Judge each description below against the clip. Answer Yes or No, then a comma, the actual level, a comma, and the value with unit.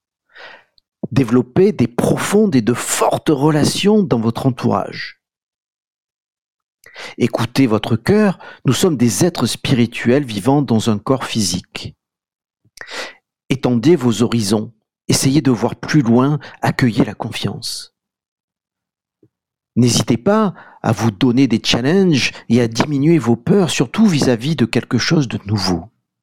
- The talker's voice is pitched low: Yes, low, 125 Hz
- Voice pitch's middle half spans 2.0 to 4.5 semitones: No, average, 5.0 semitones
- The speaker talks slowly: Yes, slow, 120 wpm